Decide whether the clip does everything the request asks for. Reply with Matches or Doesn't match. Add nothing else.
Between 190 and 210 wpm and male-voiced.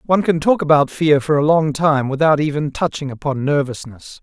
Matches